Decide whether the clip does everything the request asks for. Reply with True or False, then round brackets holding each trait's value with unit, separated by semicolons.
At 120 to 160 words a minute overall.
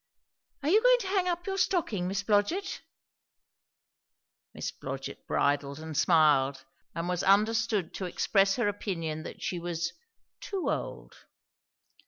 True (135 wpm)